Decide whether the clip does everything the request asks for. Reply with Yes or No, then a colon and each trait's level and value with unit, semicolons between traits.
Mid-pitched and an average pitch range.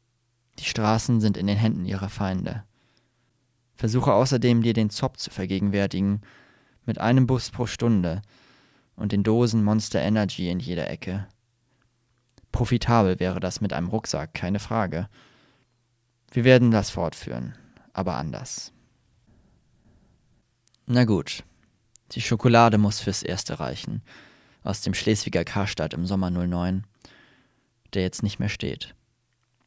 No: low, 110 Hz; average, 3.5 semitones